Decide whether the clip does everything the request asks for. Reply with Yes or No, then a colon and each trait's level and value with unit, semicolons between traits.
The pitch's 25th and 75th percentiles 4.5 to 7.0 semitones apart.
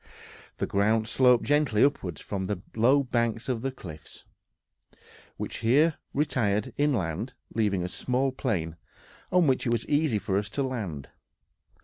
Yes: average, 4.9 semitones